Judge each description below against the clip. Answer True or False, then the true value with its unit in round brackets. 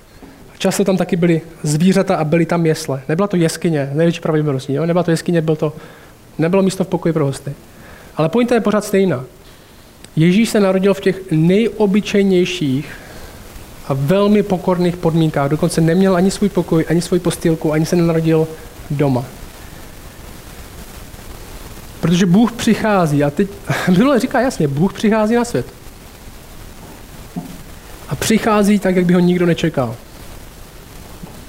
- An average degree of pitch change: True (4.0 semitones)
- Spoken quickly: False (140 wpm)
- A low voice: False (170 Hz)